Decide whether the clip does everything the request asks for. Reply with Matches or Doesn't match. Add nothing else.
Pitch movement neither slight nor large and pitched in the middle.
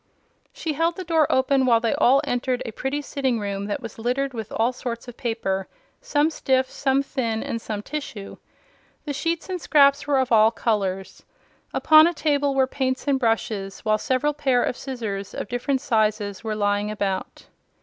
Doesn't match